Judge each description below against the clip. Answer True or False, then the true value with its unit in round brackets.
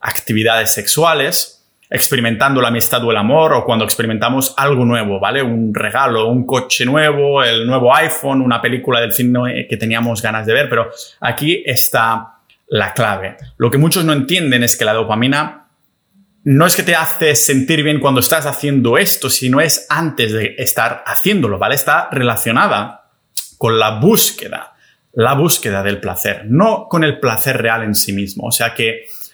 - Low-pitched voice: True (125 Hz)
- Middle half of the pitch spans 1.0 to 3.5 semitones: False (4.0 semitones)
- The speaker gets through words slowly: False (170 wpm)